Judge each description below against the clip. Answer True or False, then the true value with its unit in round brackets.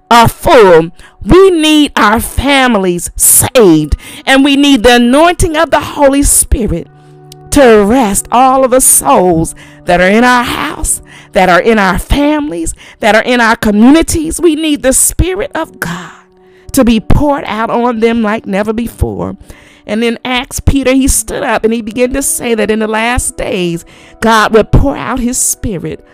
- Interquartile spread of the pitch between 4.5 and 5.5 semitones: True (5.0 semitones)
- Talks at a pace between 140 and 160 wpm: False (170 wpm)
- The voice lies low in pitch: False (240 Hz)